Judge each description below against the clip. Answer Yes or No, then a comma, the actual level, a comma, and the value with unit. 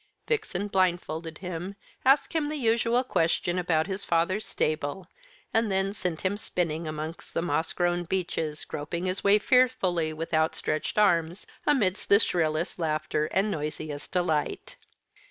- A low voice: No, medium, 175 Hz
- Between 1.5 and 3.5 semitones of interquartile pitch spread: No, average, 4.0 semitones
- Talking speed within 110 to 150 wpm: Yes, slow, 135 wpm